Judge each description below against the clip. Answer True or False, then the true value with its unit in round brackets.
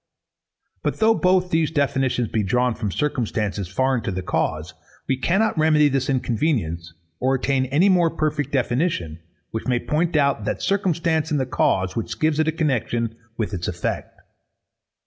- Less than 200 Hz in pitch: True (135 Hz)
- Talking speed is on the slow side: False (165 wpm)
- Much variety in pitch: True (5.9 semitones)